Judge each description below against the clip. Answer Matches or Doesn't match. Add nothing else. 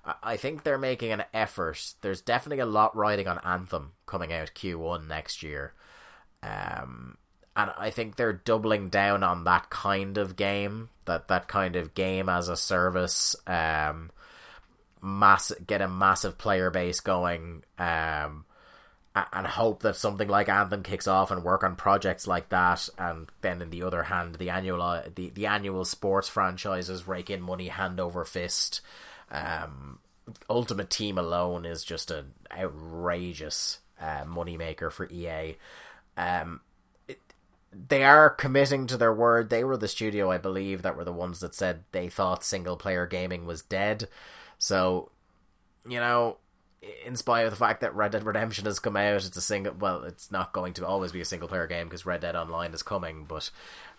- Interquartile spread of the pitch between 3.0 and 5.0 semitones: Doesn't match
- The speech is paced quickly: Doesn't match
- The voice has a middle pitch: Doesn't match